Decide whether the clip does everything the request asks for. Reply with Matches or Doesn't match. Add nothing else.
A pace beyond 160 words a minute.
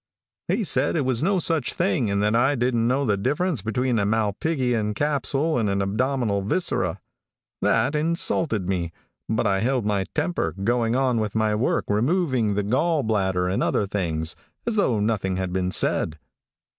Matches